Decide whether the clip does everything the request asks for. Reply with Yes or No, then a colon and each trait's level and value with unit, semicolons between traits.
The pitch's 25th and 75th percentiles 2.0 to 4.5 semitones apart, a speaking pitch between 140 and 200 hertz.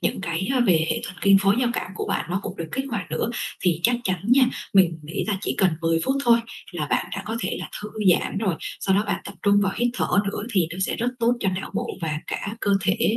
Yes: average, 4.1 semitones; high, 195 Hz